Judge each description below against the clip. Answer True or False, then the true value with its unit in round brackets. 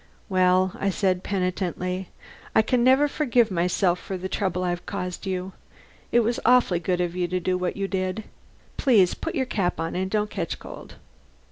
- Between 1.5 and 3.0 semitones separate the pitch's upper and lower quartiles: True (2.5 semitones)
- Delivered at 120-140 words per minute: False (180 wpm)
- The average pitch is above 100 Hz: True (185 Hz)